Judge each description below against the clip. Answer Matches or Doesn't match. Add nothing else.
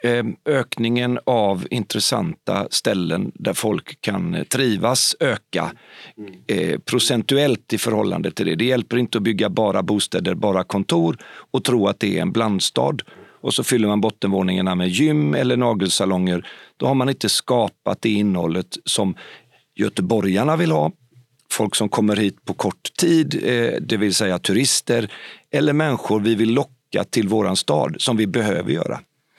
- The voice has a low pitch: Matches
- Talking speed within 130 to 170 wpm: Matches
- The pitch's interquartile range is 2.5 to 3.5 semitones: Doesn't match